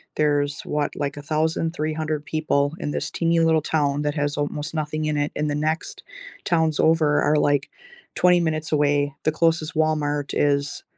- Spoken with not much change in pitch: Yes, narrow, 1.5 semitones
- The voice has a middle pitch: Yes, medium, 150 Hz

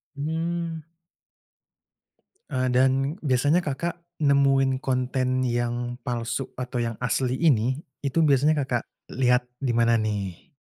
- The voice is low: Yes, low, 130 Hz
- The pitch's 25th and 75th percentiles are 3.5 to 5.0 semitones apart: No, average, 2.7 semitones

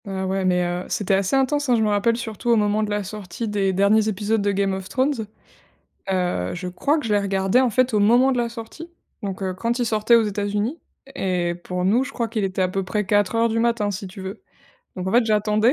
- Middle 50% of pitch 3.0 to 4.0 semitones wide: Yes, average, 3.3 semitones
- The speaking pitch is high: Yes, high, 210 Hz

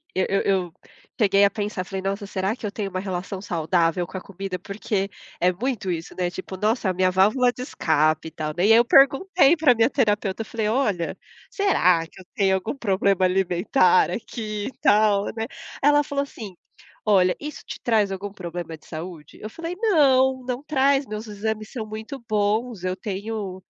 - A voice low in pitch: No, high, 205 Hz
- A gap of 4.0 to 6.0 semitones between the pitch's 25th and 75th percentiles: Yes, average, 4.4 semitones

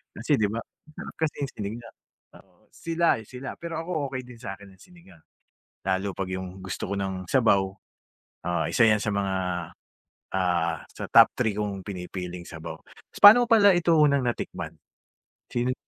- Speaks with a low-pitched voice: Yes, low, 105 Hz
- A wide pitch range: Yes, wide, 7.1 semitones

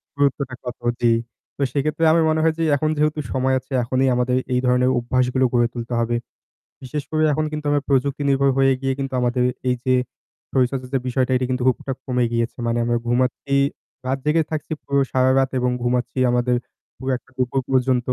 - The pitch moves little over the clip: Yes, narrow, 1.9 semitones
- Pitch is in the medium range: No, low, 130 Hz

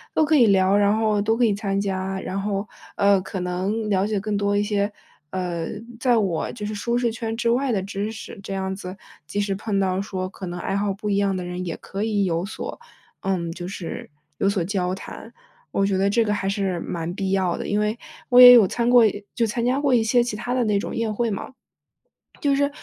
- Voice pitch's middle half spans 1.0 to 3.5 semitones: Yes, average, 2.7 semitones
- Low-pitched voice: No, high, 200 Hz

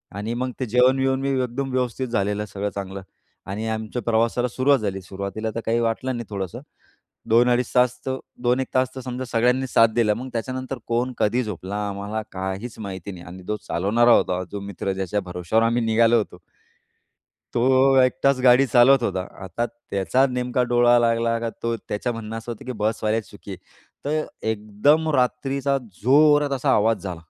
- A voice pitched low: Yes, low, 115 Hz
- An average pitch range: Yes, average, 3.7 semitones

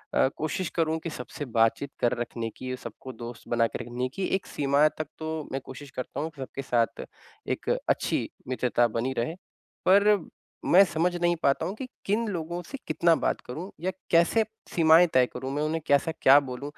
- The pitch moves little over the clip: No, average, 5.0 semitones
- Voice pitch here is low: No, medium, 145 Hz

